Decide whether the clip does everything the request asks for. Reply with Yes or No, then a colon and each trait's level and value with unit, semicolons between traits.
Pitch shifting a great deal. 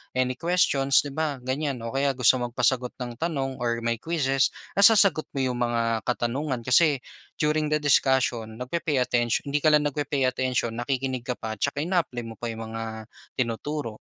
No: average, 3.7 semitones